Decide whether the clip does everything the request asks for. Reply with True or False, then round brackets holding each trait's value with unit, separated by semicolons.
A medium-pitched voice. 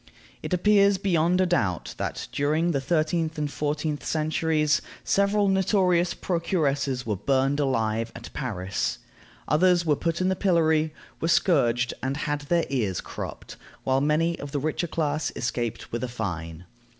True (150 Hz)